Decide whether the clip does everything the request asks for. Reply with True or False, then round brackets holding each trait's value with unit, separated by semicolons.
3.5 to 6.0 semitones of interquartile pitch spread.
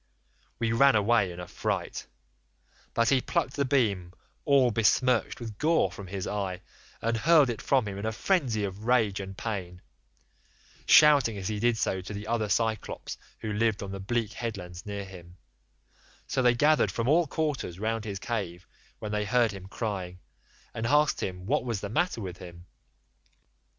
True (3.9 semitones)